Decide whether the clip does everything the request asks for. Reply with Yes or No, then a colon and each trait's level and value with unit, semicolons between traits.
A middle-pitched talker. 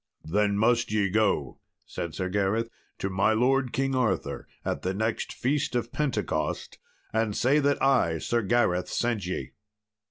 No: low, 110 Hz